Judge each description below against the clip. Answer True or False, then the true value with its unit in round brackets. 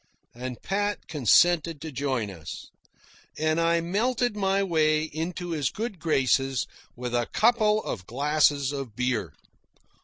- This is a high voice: False (155 Hz)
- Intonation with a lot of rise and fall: True (5.9 semitones)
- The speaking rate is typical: False (130 wpm)